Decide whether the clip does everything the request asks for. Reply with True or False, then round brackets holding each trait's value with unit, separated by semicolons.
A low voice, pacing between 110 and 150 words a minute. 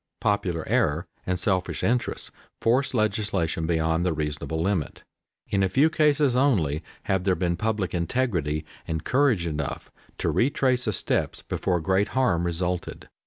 True (95 Hz; 145 wpm)